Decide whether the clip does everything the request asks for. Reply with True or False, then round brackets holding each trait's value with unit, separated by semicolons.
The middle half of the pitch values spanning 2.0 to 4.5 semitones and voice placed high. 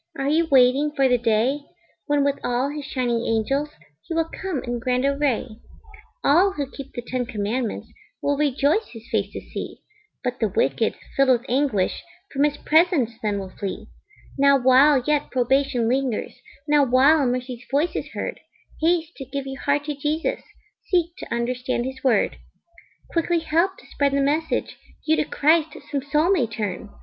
True (3.3 semitones; 275 Hz)